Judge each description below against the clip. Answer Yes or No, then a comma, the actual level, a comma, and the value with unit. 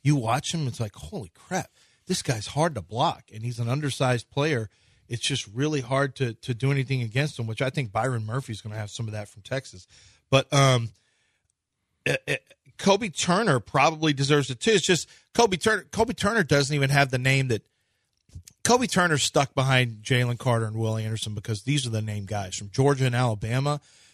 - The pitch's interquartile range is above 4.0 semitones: Yes, average, 4.4 semitones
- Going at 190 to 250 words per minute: Yes, average, 200 wpm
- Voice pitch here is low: Yes, low, 130 Hz